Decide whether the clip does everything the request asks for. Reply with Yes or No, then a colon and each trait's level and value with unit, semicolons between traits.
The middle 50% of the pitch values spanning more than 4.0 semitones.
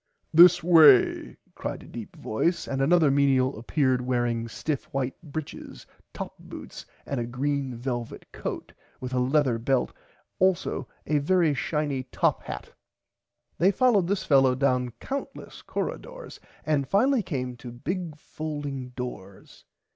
Yes: average, 4.4 semitones